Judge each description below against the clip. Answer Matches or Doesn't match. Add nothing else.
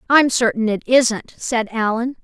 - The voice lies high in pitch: Matches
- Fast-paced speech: Doesn't match